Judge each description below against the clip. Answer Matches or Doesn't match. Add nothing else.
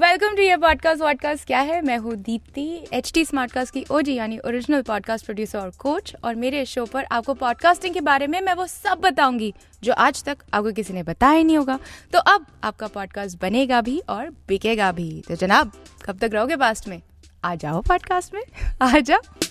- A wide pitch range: Matches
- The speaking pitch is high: Matches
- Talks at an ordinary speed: Doesn't match